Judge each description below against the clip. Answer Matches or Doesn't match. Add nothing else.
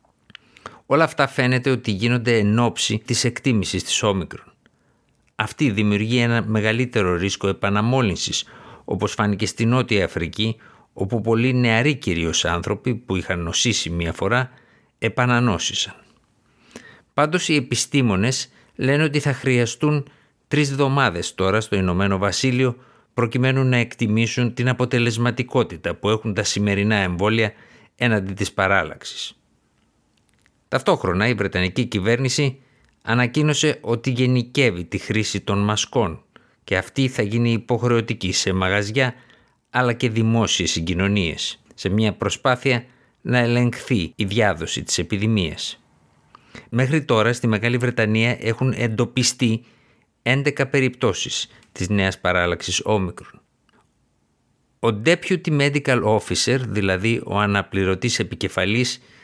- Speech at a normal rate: Doesn't match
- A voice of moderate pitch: Doesn't match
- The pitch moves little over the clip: Doesn't match